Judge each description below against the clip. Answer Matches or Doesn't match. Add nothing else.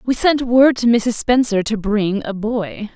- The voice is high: Matches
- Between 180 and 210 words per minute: Matches